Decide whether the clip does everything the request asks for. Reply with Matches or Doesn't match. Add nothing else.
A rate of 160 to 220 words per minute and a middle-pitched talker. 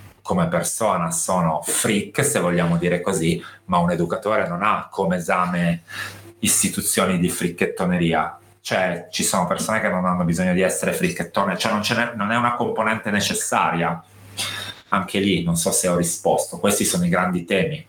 Doesn't match